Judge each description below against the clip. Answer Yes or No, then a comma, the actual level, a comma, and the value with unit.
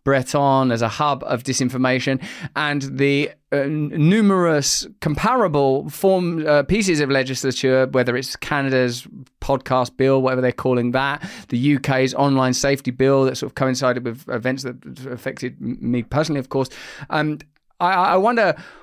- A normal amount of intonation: No, narrow, 2.2 semitones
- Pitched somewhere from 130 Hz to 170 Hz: Yes, low, 135 Hz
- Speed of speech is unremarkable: Yes, average, 150 wpm